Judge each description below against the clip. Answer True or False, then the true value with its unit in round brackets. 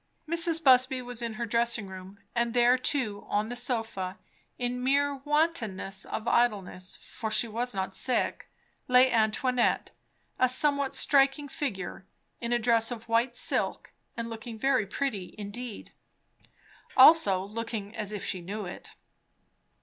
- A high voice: True (235 Hz)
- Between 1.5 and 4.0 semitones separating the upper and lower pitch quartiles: True (3.5 semitones)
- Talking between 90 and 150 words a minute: True (140 wpm)